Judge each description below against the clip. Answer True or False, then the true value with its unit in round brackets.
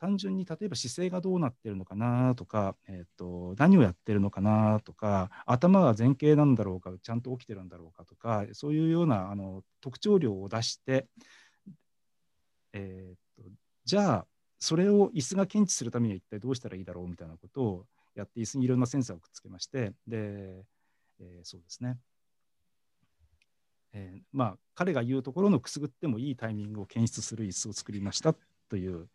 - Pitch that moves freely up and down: True (6.4 semitones)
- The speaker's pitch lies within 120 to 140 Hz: False (110 Hz)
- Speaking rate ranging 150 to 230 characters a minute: False (380 characters per minute)